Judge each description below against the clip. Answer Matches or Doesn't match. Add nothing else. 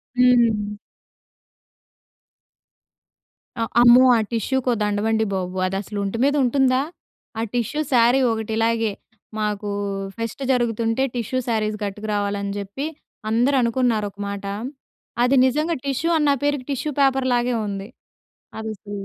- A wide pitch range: Doesn't match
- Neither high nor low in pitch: Doesn't match